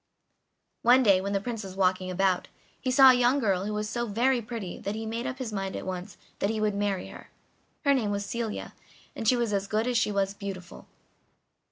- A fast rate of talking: Yes, fast, 225 wpm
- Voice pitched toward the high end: Yes, high, 210 Hz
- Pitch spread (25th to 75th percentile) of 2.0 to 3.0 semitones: No, average, 3.5 semitones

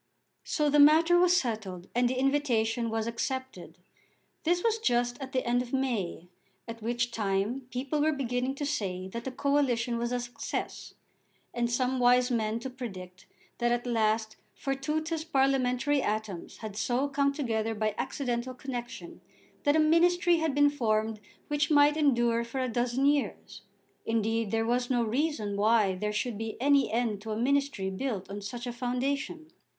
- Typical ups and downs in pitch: Yes, average, 3.9 semitones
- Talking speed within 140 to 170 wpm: Yes, average, 165 wpm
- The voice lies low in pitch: No, high, 245 Hz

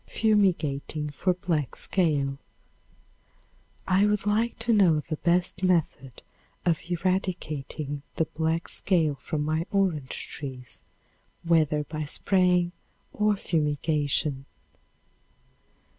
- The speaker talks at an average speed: No, slow, 100 wpm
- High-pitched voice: No, medium, 165 Hz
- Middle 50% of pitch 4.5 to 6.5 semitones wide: No, average, 3.7 semitones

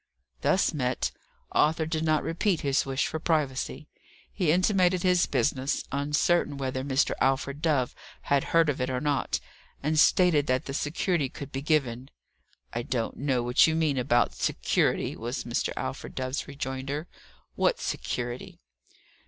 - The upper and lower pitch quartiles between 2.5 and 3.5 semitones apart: Yes, average, 3.2 semitones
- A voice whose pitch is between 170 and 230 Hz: No, medium, 145 Hz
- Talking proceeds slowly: No, average, 150 wpm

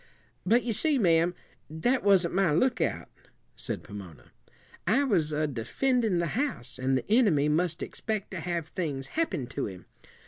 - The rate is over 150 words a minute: Yes, average, 160 wpm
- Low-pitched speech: No, medium, 175 Hz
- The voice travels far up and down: Yes, wide, 7.0 semitones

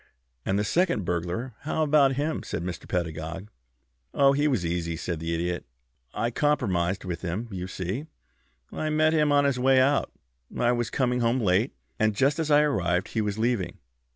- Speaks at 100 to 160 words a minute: No, average, 180 wpm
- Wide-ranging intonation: Yes, wide, 8.0 semitones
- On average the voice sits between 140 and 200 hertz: No, low, 115 Hz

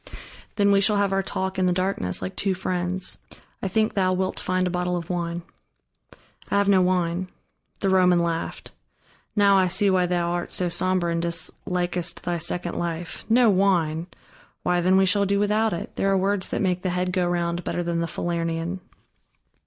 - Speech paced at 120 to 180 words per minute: No, average, 190 wpm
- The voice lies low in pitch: No, medium, 180 Hz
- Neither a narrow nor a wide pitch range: No, narrow, 1.8 semitones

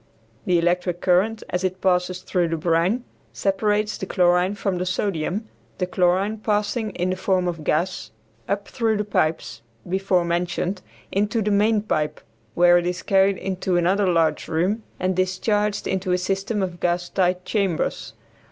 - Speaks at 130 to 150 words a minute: No, average, 160 wpm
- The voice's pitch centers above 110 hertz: Yes, medium, 185 Hz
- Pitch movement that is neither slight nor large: No, narrow, 2.3 semitones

